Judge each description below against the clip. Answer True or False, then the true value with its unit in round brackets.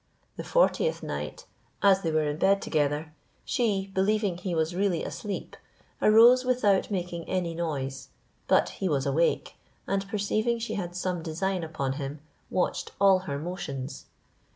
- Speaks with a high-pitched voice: False (180 Hz)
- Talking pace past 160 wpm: False (150 wpm)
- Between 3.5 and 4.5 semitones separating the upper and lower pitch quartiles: True (4.1 semitones)